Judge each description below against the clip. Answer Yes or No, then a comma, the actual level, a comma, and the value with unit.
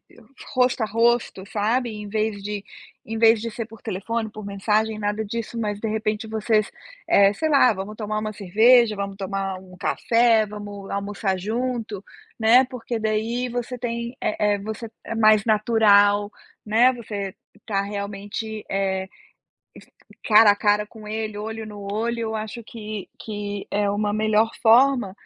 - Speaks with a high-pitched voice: Yes, high, 215 Hz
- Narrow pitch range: Yes, narrow, 1.9 semitones